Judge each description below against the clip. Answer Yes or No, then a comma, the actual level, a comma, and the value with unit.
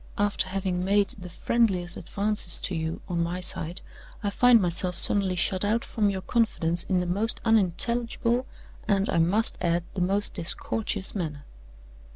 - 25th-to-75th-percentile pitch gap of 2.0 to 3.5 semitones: Yes, average, 3.1 semitones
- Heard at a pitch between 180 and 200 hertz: Yes, high, 190 Hz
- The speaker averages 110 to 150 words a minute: No, average, 160 wpm